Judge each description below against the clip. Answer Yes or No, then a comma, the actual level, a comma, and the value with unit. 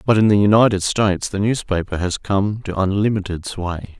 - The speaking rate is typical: Yes, average, 180 wpm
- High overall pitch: No, low, 100 Hz